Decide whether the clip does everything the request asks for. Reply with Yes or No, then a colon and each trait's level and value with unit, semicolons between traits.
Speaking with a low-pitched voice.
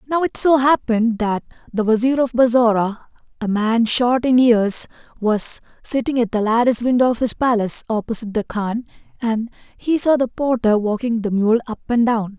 No: high, 235 Hz